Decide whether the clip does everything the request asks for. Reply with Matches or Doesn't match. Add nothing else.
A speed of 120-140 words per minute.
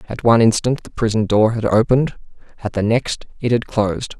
Doesn't match